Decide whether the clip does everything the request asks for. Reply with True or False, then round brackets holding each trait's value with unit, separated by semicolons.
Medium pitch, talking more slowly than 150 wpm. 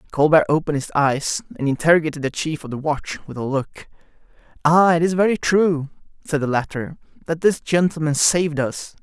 False (155 Hz; 175 wpm)